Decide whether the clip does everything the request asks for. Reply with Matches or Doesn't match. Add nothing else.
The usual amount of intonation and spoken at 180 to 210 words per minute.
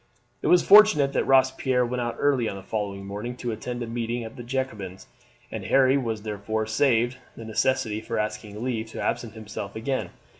Matches